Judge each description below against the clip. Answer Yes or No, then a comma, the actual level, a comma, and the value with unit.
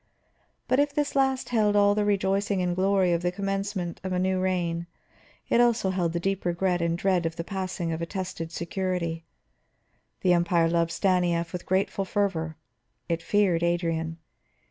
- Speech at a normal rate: Yes, average, 170 wpm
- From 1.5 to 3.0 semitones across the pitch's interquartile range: Yes, narrow, 2.5 semitones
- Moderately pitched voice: Yes, medium, 180 Hz